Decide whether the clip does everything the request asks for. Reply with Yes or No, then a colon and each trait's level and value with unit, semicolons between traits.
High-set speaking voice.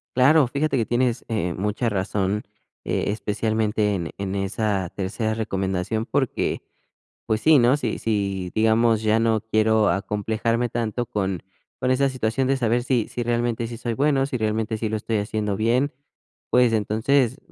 No: low, 110 Hz